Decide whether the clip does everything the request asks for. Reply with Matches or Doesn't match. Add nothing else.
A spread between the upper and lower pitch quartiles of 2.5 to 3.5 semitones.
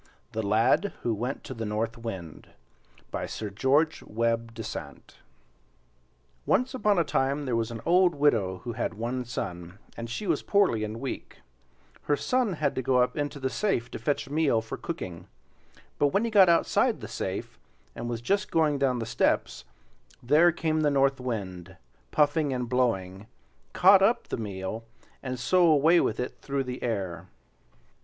Doesn't match